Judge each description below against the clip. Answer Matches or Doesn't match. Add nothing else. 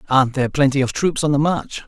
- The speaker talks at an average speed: Doesn't match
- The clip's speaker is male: Matches